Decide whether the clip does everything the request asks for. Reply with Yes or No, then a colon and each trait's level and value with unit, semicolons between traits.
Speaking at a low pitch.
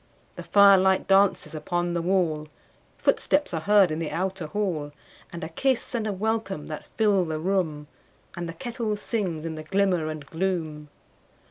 No: medium, 180 Hz